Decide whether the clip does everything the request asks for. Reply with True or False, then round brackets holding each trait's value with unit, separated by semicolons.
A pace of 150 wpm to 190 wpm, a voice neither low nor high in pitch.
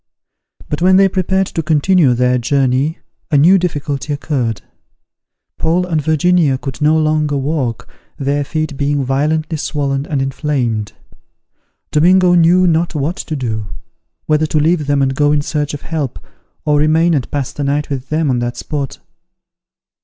True (160 wpm; 150 Hz)